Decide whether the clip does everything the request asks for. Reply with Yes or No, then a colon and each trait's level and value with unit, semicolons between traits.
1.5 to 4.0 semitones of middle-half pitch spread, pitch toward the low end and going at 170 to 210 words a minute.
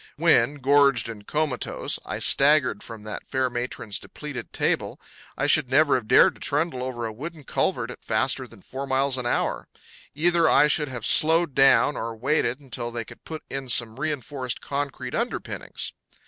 Yes: average, 3.6 semitones; low, 130 Hz; average, 175 wpm